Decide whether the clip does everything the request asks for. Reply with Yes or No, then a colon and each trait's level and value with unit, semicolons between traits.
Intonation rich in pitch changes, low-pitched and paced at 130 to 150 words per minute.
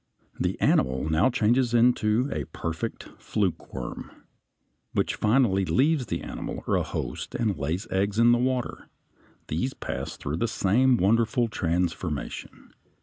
Yes: wide, 5.9 semitones; low, 105 Hz; slow, 135 wpm